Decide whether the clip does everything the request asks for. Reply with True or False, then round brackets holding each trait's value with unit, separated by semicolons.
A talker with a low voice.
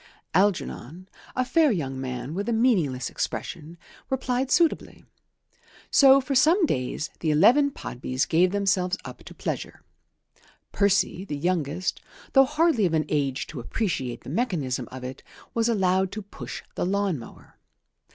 False (185 Hz)